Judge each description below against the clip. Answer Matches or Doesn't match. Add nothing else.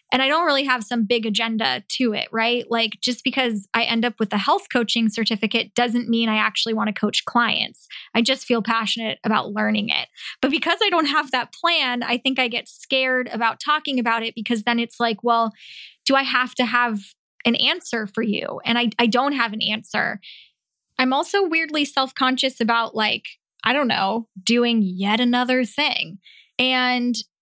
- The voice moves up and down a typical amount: Doesn't match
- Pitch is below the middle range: Doesn't match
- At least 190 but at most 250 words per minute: Matches